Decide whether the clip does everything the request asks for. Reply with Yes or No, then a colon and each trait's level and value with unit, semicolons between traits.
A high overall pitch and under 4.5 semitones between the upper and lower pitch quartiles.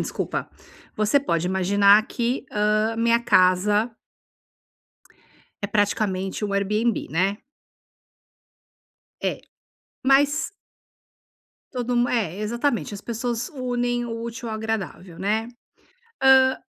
Yes: high, 220 Hz; average, 3.1 semitones